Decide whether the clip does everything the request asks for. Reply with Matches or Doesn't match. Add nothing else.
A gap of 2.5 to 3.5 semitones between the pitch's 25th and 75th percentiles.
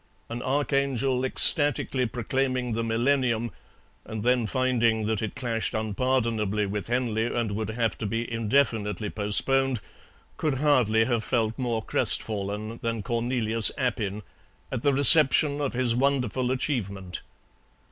Matches